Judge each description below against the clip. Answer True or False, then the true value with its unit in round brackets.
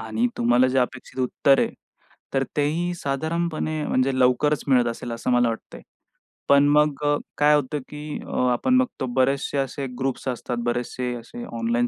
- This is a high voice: False (135 Hz)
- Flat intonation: False (3.2 semitones)